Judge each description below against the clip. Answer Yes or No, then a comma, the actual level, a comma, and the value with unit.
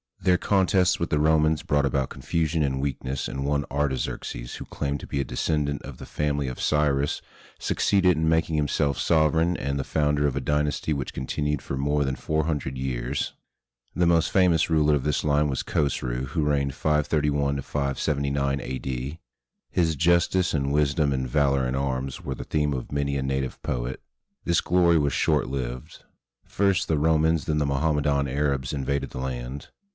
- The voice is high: No, very low, 70 Hz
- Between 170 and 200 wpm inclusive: Yes, average, 175 wpm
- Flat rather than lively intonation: Yes, narrow, 2.3 semitones